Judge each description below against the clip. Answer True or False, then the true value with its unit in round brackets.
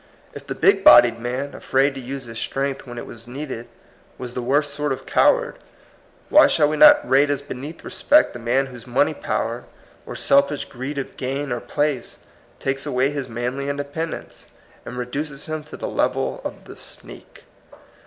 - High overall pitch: False (135 Hz)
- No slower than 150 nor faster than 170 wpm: False (185 wpm)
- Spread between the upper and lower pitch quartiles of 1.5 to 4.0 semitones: True (2.8 semitones)